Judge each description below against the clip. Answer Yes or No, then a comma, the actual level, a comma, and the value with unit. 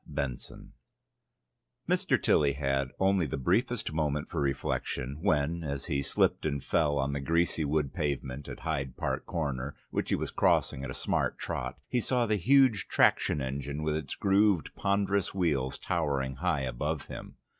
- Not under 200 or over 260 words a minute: No, average, 165 wpm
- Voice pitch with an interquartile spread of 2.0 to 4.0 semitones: No, average, 4.5 semitones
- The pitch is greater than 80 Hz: No, very low, 75 Hz